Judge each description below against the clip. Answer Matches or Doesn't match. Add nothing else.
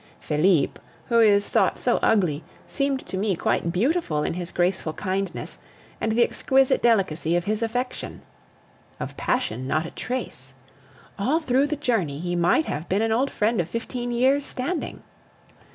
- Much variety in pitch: Matches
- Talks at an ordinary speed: Matches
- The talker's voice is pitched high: Matches